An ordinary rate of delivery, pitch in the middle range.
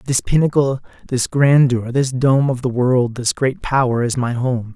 No: average, 190 wpm; low, 130 Hz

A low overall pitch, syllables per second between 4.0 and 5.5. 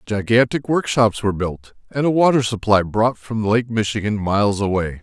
Yes: low, 110 Hz; 5.0 syllables/s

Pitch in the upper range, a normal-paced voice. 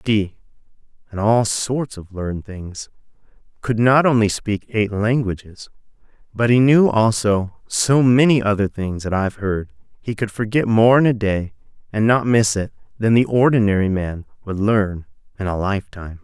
No: low, 110 Hz; average, 160 wpm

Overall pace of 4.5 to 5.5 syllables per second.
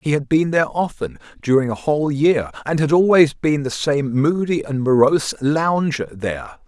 Yes: 4.9 syllables/s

